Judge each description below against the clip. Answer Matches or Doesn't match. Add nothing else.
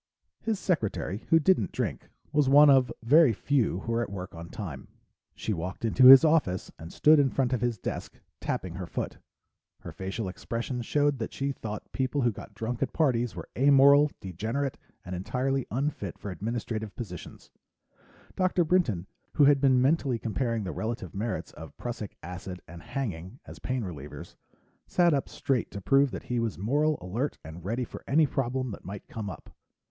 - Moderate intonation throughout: Doesn't match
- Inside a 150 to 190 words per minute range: Matches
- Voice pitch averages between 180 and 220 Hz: Doesn't match